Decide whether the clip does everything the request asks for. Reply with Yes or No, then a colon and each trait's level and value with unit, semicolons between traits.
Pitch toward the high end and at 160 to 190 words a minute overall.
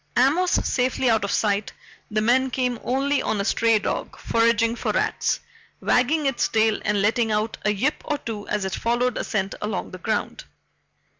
Yes: high, 230 Hz; average, 180 wpm